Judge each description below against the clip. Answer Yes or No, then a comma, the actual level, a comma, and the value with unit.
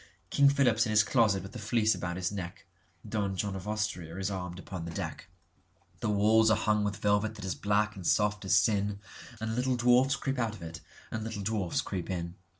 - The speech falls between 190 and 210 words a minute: Yes, average, 200 wpm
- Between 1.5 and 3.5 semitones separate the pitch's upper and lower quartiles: Yes, average, 2.8 semitones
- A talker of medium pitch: No, low, 105 Hz